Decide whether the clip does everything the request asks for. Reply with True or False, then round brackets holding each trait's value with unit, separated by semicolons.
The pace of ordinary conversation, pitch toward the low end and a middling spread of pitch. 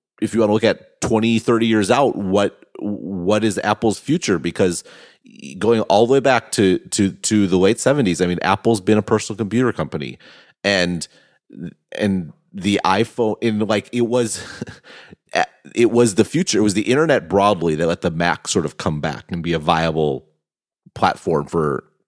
True (180 wpm; 105 Hz; 4.1 semitones)